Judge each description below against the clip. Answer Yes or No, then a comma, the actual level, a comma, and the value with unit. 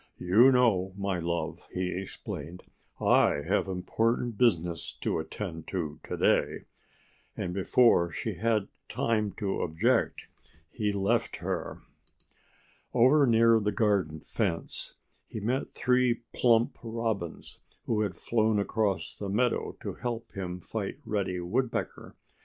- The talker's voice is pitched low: Yes, low, 105 Hz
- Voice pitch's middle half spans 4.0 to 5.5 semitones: Yes, average, 4.3 semitones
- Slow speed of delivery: Yes, slow, 125 wpm